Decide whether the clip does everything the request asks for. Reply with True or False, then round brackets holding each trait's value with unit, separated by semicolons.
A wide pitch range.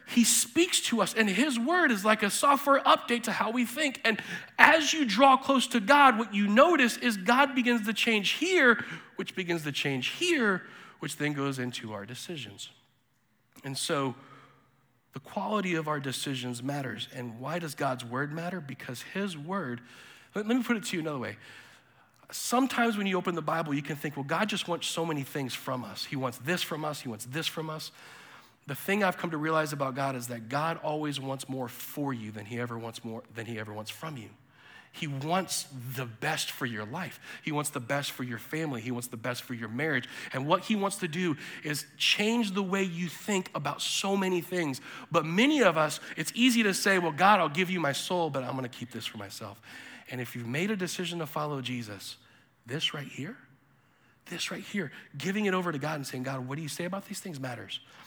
True (7.4 semitones)